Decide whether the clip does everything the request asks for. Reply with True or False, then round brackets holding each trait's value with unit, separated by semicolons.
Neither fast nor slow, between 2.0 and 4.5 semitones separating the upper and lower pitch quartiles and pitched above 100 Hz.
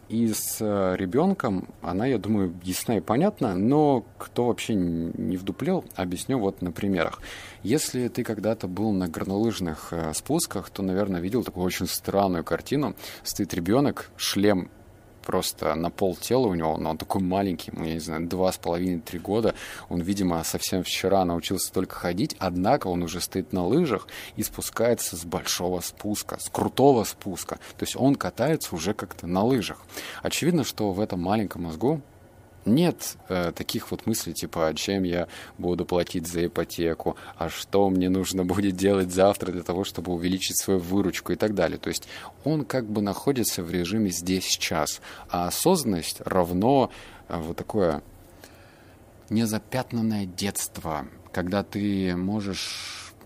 False (150 wpm; 3.3 semitones; 95 Hz)